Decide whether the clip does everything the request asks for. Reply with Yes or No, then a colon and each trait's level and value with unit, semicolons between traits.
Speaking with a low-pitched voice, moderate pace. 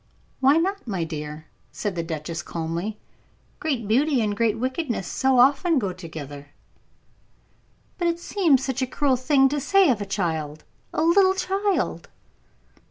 No: very high, 250 Hz; average, 150 wpm